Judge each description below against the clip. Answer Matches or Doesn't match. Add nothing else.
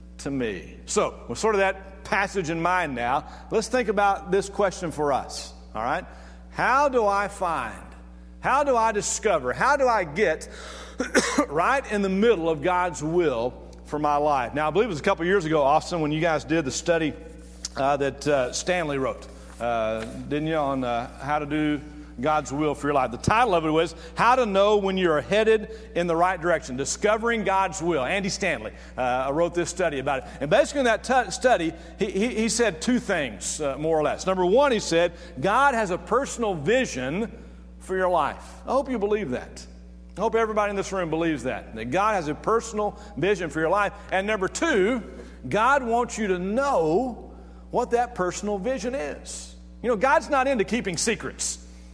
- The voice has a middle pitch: Matches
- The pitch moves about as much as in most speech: Doesn't match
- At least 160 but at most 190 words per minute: Doesn't match